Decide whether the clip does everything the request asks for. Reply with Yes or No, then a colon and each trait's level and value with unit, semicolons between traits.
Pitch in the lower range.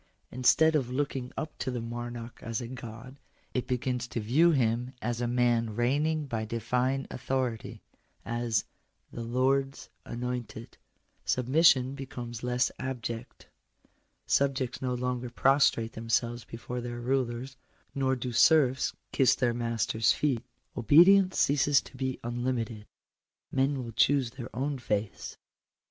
Yes: low, 125 Hz